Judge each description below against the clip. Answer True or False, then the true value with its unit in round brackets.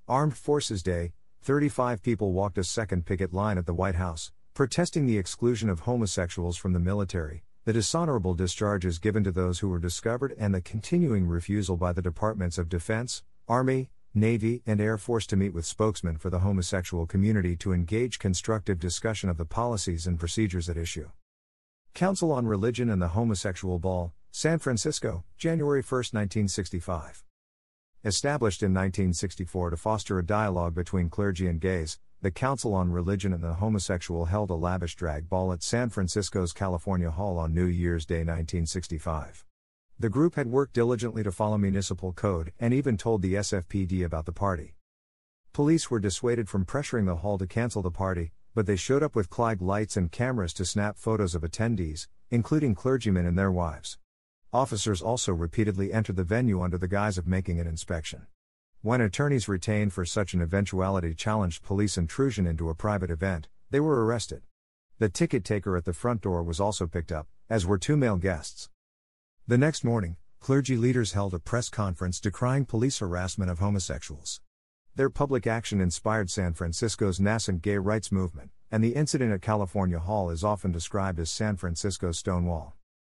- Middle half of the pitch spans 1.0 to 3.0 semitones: False (4.0 semitones)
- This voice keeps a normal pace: True (175 wpm)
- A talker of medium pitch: False (95 Hz)